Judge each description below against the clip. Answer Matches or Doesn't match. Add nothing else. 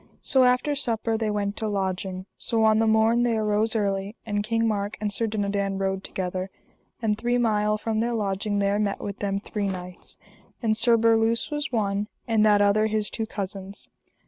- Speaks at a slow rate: Doesn't match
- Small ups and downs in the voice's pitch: Matches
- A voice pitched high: Matches